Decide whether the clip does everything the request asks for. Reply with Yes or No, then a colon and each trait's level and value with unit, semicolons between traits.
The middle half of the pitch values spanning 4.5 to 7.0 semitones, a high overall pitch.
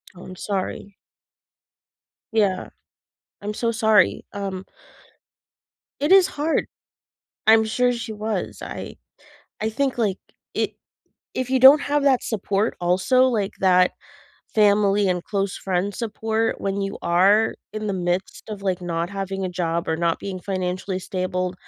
No: average, 3.2 semitones; high, 200 Hz